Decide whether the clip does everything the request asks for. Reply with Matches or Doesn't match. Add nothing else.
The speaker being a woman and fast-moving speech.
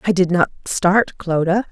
Doesn't match